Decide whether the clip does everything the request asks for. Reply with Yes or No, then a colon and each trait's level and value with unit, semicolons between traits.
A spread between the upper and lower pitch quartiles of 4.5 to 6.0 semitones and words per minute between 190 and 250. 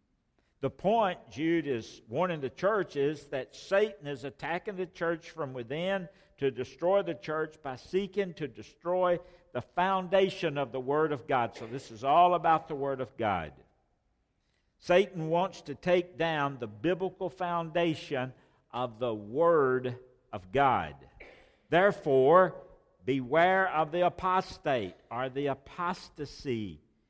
No: average, 5.1 semitones; slow, 135 wpm